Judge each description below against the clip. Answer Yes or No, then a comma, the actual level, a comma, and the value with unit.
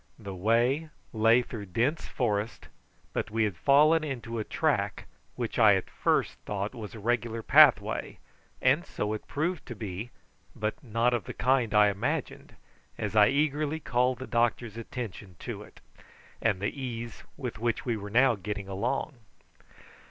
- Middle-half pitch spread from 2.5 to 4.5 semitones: Yes, average, 3.5 semitones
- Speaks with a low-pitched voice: Yes, low, 115 Hz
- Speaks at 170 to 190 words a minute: No, average, 160 wpm